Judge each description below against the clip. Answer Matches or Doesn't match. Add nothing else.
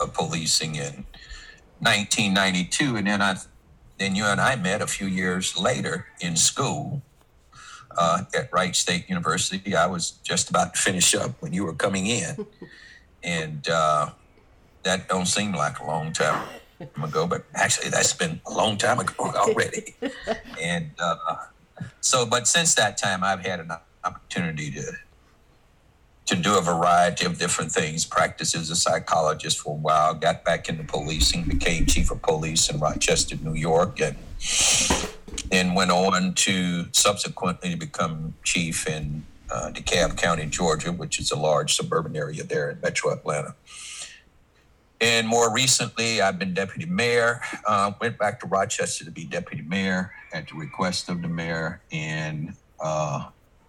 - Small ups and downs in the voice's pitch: Doesn't match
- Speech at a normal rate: Matches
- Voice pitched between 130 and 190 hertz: Doesn't match